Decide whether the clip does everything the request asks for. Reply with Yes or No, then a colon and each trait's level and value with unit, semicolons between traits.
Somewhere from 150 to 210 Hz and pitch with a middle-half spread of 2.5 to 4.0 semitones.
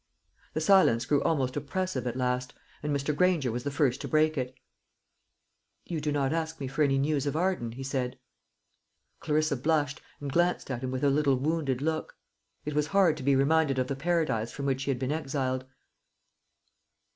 No: medium, 140 Hz; average, 3.2 semitones